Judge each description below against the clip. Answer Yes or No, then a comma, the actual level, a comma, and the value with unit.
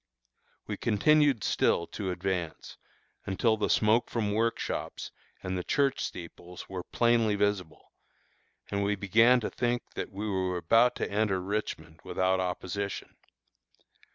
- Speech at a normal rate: No, slow, 130 wpm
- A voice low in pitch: Yes, low, 100 Hz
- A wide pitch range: No, average, 3.6 semitones